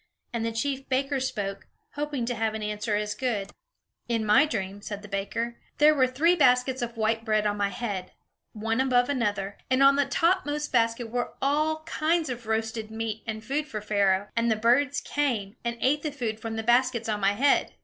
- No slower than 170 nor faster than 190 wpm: No, average, 200 wpm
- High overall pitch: Yes, high, 235 Hz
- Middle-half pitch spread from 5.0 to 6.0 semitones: No, average, 4.1 semitones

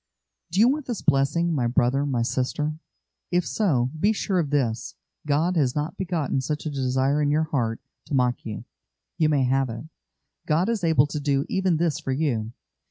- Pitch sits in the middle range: Yes, medium, 145 Hz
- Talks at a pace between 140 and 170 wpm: No, average, 190 wpm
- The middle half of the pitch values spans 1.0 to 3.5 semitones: No, average, 4.2 semitones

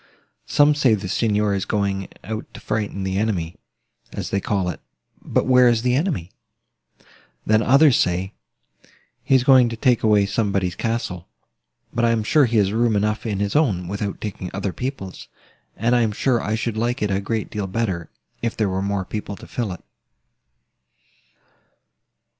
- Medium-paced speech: Yes, average, 175 wpm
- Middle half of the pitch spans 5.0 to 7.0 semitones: No, average, 3.3 semitones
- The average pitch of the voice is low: Yes, low, 105 Hz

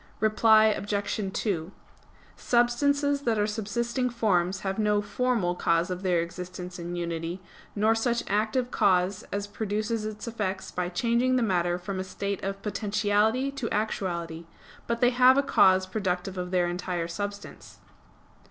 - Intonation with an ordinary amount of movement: Yes, average, 3.9 semitones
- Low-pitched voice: No, high, 205 Hz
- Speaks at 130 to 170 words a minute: Yes, average, 150 wpm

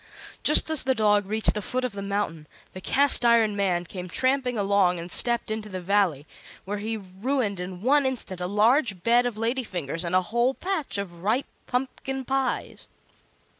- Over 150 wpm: Yes, average, 185 wpm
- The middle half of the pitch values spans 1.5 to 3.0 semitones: No, average, 5.1 semitones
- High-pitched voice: Yes, high, 210 Hz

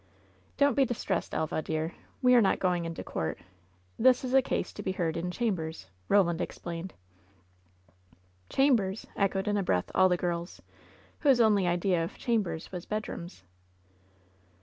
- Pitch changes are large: No, average, 4.6 semitones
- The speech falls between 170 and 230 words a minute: No, average, 155 wpm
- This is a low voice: No, medium, 185 Hz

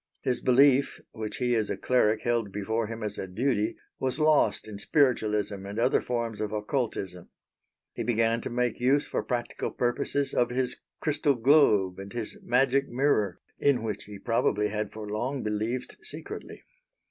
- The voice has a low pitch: Yes, low, 115 Hz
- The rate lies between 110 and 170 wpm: Yes, average, 165 wpm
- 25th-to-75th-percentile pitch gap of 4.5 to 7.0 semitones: No, average, 3.3 semitones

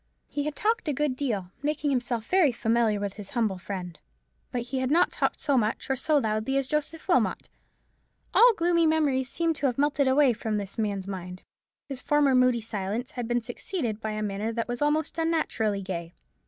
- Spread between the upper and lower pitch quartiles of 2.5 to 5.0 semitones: No, wide, 5.6 semitones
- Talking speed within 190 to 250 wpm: Yes, average, 195 wpm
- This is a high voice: Yes, very high, 250 Hz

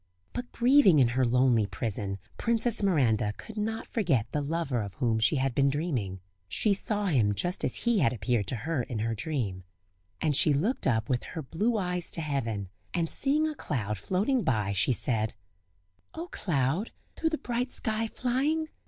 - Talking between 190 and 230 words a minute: No, average, 180 wpm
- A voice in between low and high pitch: Yes, medium, 145 Hz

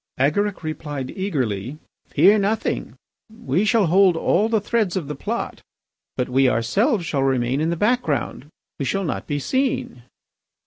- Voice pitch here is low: No, medium, 165 Hz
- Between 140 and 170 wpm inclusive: Yes, average, 150 wpm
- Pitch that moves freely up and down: Yes, wide, 7.4 semitones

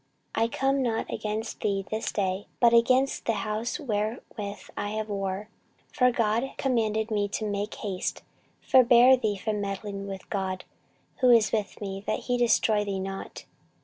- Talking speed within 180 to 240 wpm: No, average, 160 wpm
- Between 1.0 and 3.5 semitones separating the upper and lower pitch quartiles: Yes, average, 2.7 semitones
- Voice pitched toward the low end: No, high, 215 Hz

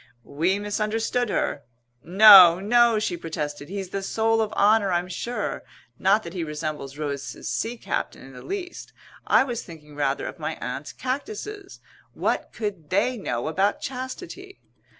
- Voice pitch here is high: Yes, high, 200 Hz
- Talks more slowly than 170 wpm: Yes, average, 150 wpm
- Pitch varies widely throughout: Yes, wide, 6.2 semitones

